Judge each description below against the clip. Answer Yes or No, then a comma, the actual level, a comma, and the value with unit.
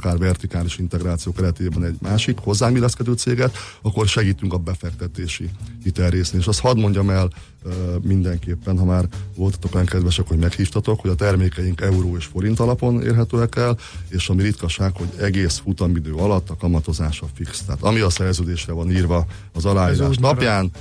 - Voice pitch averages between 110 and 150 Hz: No, very low, 95 Hz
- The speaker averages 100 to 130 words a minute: No, fast, 155 wpm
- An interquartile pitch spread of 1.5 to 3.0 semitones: Yes, average, 2.7 semitones